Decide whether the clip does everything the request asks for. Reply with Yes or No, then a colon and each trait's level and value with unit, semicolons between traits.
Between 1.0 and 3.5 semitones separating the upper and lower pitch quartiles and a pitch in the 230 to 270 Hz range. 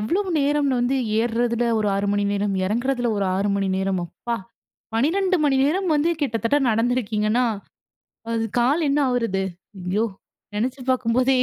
No: average, 4.2 semitones; high, 240 Hz